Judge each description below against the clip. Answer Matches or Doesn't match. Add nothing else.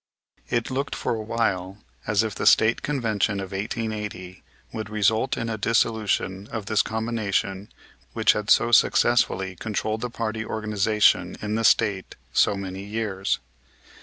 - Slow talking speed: Doesn't match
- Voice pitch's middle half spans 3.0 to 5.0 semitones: Doesn't match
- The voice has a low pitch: Matches